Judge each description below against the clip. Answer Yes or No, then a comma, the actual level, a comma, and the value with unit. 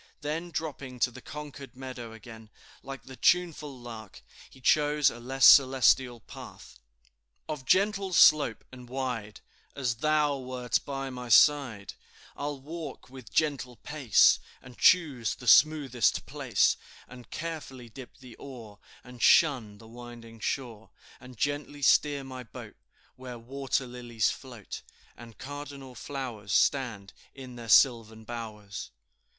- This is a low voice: Yes, low, 130 Hz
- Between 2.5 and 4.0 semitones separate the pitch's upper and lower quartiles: Yes, average, 3.3 semitones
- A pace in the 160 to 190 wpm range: No, slow, 135 wpm